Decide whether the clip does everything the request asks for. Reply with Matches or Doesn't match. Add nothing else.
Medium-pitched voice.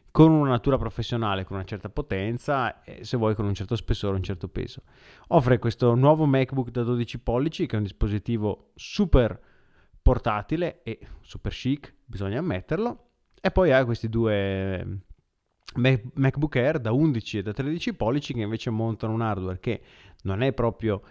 Doesn't match